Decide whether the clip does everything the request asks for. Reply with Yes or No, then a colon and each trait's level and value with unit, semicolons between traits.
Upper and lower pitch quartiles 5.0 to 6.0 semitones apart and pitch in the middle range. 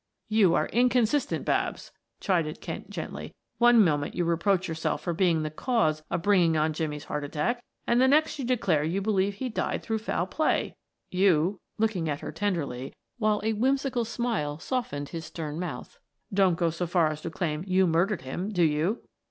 Yes: wide, 5.6 semitones; medium, 180 Hz